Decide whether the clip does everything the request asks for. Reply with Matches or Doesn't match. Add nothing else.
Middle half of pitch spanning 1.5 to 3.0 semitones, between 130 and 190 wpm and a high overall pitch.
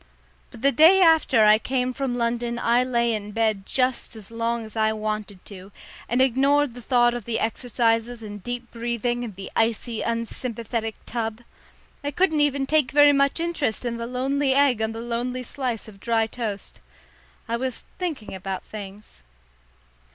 Matches